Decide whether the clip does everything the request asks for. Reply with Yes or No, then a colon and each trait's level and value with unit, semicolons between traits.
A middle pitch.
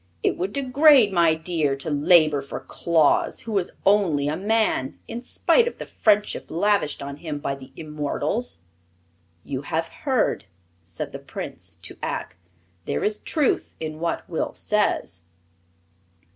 Yes: medium, 165 Hz